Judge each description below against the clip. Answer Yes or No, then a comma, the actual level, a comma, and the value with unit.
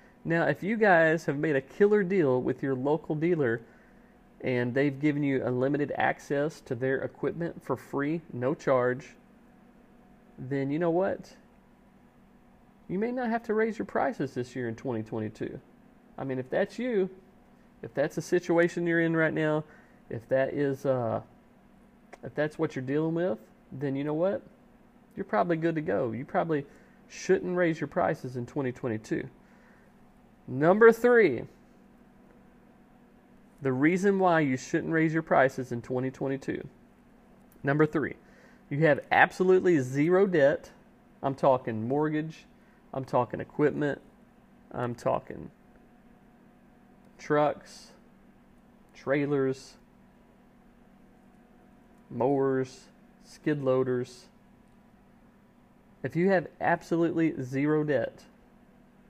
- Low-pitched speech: No, medium, 170 Hz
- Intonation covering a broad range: Yes, wide, 8.7 semitones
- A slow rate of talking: Yes, slow, 120 wpm